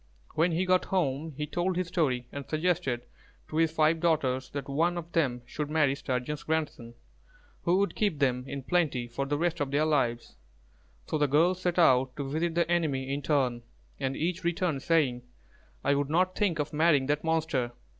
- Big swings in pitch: No, average, 4.0 semitones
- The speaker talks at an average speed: Yes, average, 190 wpm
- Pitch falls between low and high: Yes, medium, 150 Hz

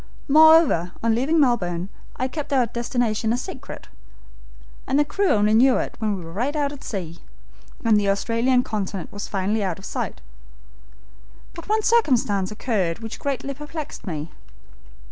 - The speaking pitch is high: Yes, high, 230 Hz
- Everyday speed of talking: Yes, average, 160 wpm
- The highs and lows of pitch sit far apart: Yes, wide, 6.0 semitones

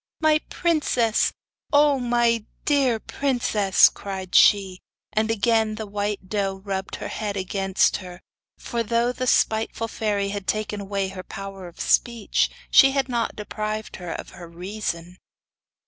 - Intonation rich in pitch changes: No, average, 3.4 semitones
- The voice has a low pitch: No, high, 210 Hz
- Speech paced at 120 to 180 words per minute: Yes, average, 145 wpm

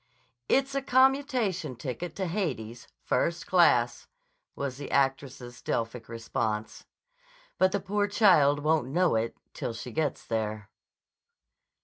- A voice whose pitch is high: No, medium, 145 Hz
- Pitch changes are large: Yes, wide, 7.9 semitones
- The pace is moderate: No, slow, 120 wpm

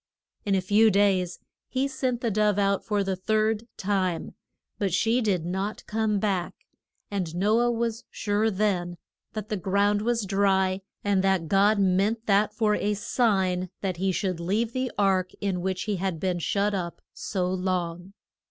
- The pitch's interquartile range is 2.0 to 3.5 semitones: Yes, narrow, 2.4 semitones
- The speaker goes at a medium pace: Yes, average, 170 wpm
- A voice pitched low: No, high, 200 Hz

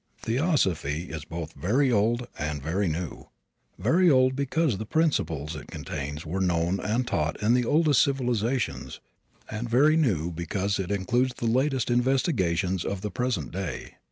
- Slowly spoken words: No, average, 155 wpm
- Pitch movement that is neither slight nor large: No, wide, 7.3 semitones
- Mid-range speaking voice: No, low, 105 Hz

